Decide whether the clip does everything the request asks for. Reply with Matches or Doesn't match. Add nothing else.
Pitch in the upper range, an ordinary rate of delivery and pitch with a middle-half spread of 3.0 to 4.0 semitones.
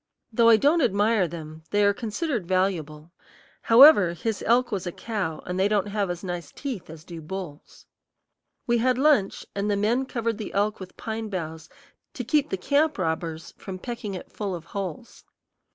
Doesn't match